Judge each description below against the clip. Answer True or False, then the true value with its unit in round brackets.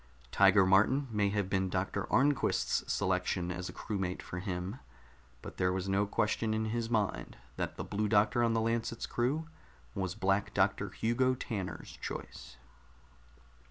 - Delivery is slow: False (155 wpm)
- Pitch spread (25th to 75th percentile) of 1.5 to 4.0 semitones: True (3.2 semitones)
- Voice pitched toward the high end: False (105 Hz)